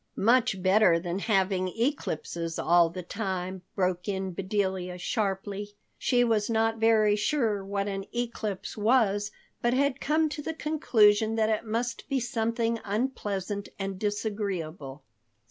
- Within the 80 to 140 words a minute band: Yes, slow, 135 wpm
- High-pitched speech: Yes, high, 205 Hz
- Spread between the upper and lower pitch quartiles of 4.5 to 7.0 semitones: No, average, 3.3 semitones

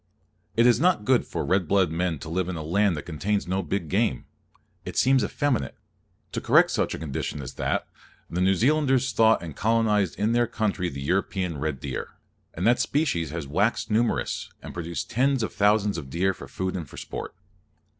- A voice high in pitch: No, very low, 95 Hz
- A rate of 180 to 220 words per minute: Yes, average, 200 wpm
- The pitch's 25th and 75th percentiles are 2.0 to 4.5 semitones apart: No, wide, 5.4 semitones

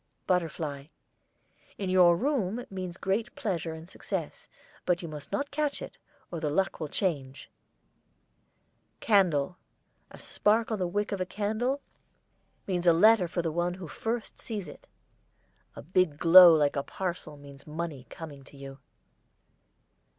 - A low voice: No, medium, 175 Hz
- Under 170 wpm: Yes, average, 150 wpm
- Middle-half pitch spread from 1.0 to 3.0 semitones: No, average, 4.5 semitones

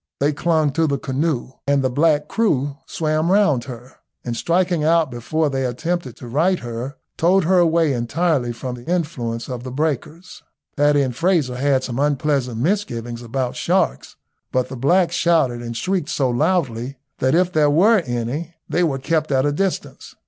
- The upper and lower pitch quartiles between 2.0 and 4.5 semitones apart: No, average, 4.9 semitones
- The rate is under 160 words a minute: No, average, 175 wpm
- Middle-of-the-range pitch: Yes, medium, 145 Hz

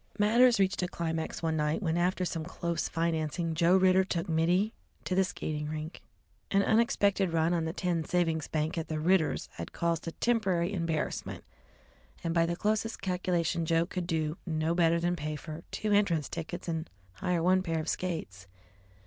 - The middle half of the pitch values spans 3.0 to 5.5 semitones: No, narrow, 2.5 semitones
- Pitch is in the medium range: Yes, medium, 170 Hz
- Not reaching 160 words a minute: No, average, 180 wpm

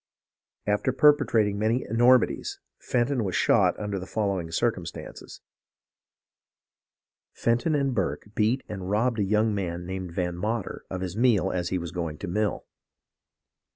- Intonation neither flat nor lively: Yes, average, 4.2 semitones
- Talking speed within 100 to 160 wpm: Yes, average, 140 wpm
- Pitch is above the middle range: No, low, 105 Hz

